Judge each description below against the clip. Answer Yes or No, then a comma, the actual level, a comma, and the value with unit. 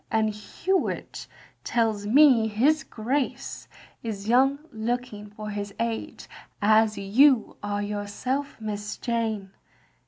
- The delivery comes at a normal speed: No, slow, 105 wpm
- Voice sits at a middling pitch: No, high, 220 Hz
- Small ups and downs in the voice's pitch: No, average, 3.1 semitones